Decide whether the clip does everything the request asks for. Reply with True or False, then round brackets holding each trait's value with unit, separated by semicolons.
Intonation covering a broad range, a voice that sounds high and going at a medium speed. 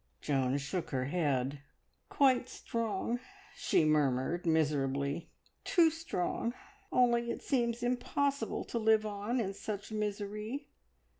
False (8.2 semitones; 210 Hz; 115 wpm)